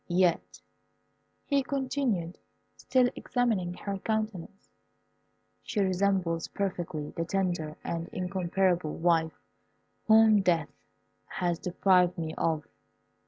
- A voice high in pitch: No, medium, 180 Hz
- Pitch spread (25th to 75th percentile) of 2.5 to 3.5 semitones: Yes, average, 3.1 semitones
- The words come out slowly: Yes, slow, 95 wpm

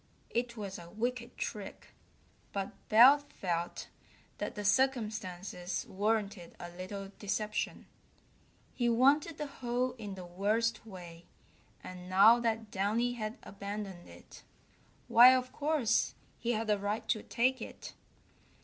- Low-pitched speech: No, high, 215 Hz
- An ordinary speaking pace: No, slow, 130 wpm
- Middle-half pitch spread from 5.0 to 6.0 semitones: No, average, 3.7 semitones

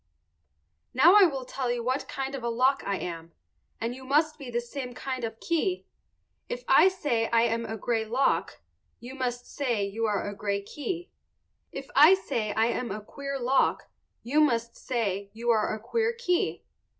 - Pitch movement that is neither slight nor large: Yes, average, 3.6 semitones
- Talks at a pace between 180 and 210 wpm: Yes, average, 190 wpm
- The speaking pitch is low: No, high, 245 Hz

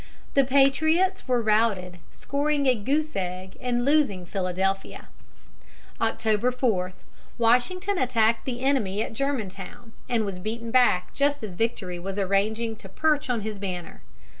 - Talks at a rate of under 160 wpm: Yes, average, 140 wpm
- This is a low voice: No, high, 225 Hz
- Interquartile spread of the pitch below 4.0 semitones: No, wide, 5.5 semitones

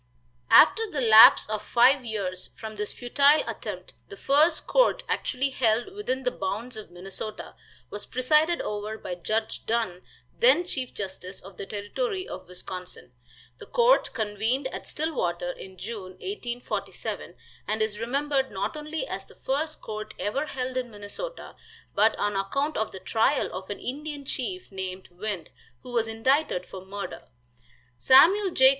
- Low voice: No, high, 230 Hz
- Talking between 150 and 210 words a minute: Yes, average, 155 wpm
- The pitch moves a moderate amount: No, wide, 5.8 semitones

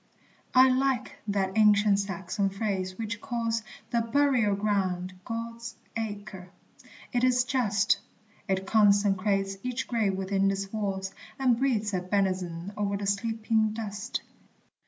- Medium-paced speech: No, slow, 125 wpm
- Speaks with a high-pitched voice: Yes, high, 205 Hz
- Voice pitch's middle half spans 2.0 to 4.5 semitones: Yes, average, 2.8 semitones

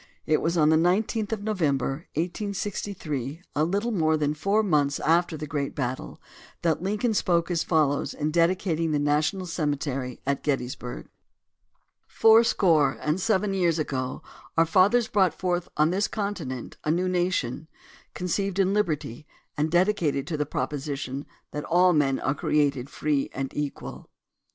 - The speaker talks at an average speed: Yes, average, 150 wpm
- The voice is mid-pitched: Yes, medium, 160 Hz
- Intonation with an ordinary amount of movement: Yes, average, 4.3 semitones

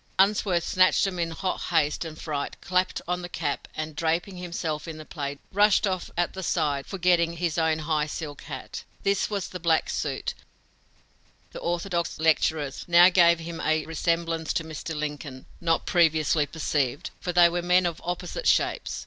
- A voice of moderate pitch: Yes, medium, 165 Hz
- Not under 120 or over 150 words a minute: No, average, 175 wpm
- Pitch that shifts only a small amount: Yes, narrow, 2.2 semitones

